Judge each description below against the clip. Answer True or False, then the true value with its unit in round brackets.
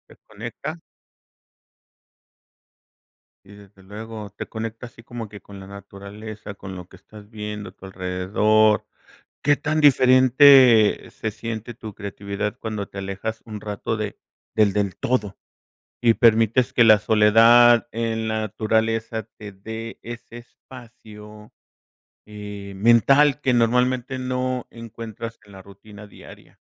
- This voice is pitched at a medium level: False (110 Hz)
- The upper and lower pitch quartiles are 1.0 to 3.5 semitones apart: True (2.4 semitones)